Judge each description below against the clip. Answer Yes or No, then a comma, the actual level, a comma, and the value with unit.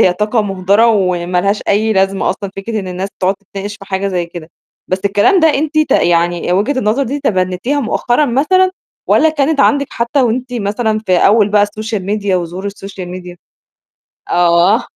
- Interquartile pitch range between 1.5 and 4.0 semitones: No, average, 4.4 semitones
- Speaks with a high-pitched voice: Yes, high, 205 Hz